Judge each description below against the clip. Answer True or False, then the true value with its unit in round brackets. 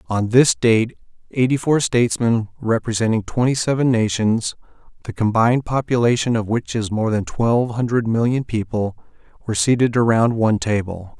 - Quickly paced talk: False (145 wpm)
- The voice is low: True (115 Hz)